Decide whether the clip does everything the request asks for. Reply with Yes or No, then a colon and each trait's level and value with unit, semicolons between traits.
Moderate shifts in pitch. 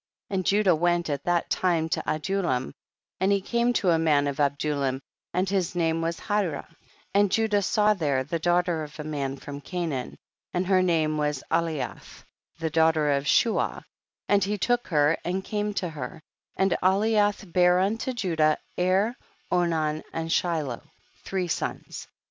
Yes: average, 4.0 semitones